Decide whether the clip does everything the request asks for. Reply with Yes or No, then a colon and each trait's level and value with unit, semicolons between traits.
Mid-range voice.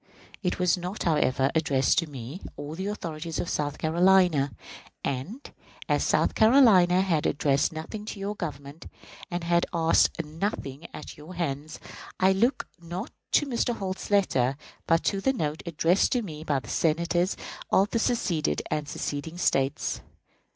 Yes: medium, 170 Hz